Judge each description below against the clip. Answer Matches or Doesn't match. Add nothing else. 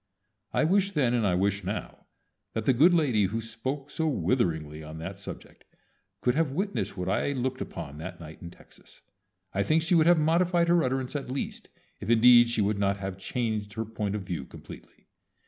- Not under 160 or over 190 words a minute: Doesn't match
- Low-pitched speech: Matches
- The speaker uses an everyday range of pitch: Doesn't match